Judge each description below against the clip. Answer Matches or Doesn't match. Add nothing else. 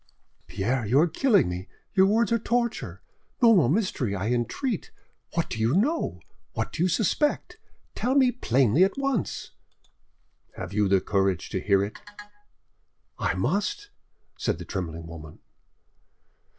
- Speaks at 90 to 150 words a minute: Matches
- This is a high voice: Doesn't match